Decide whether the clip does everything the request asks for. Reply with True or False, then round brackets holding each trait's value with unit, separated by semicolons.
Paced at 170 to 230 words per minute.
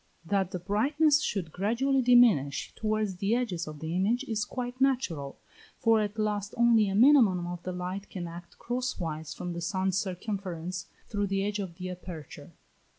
True (175 wpm)